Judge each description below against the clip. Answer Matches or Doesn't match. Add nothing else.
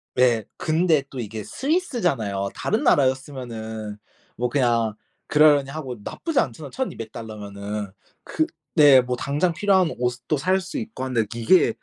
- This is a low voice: Matches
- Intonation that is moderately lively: Doesn't match